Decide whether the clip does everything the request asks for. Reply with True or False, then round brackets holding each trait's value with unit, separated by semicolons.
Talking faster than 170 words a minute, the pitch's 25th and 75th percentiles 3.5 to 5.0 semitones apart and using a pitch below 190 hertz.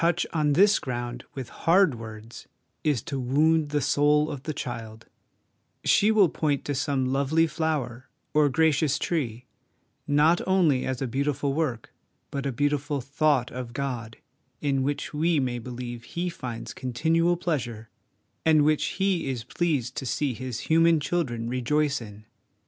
False (160 wpm; 4.2 semitones; 140 Hz)